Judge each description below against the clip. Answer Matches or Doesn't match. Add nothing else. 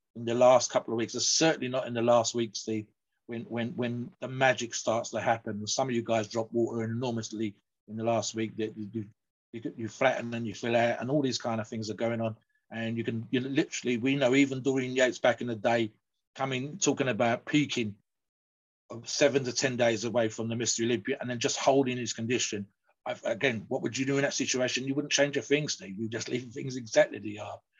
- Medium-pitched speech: Doesn't match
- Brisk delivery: Matches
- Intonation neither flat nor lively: Doesn't match